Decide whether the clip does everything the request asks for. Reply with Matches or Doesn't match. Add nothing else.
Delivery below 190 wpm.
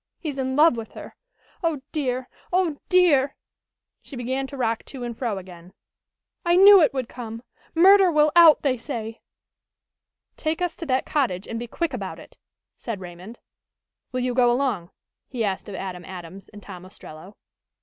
Matches